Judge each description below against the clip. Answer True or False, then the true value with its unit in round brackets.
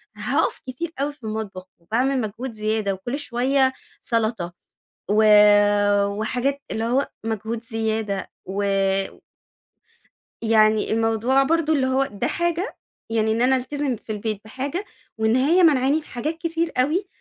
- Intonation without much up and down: False (4.2 semitones)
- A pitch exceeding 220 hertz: True (240 Hz)